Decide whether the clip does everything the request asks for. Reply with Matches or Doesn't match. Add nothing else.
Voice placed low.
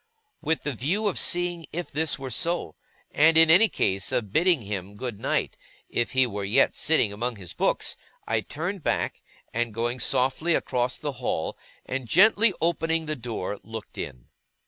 Matches